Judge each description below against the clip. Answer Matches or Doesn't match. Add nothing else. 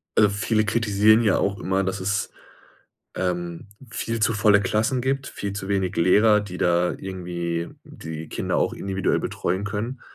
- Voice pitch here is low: Matches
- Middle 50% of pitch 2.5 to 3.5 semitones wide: Matches